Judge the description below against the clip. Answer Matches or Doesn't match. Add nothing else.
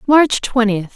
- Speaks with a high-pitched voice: Matches